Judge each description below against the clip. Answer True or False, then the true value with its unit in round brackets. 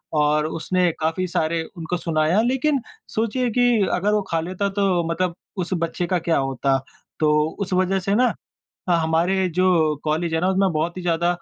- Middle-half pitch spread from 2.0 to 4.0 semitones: True (3.1 semitones)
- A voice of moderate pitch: True (175 Hz)